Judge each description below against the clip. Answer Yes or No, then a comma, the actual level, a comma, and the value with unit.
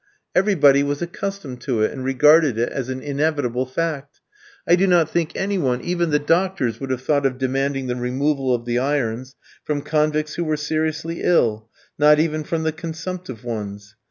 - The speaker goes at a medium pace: Yes, average, 185 wpm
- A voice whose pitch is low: No, medium, 145 Hz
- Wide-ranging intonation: No, average, 3.8 semitones